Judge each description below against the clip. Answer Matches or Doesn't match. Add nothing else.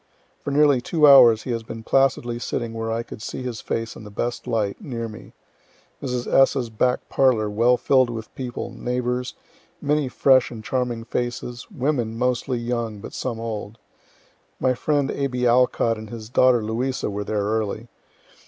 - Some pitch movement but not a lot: Doesn't match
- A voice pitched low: Matches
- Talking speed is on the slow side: Doesn't match